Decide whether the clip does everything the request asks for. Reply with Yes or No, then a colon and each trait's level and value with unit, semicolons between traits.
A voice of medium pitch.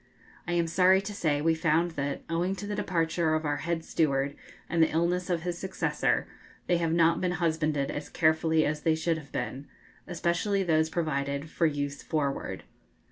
Yes: medium, 165 Hz